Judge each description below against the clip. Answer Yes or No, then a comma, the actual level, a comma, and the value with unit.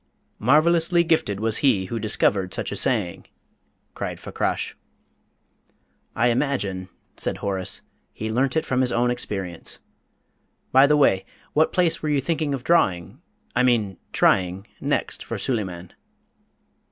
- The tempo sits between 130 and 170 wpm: Yes, average, 140 wpm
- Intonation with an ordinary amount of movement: No, wide, 6.9 semitones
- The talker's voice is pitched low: Yes, low, 120 Hz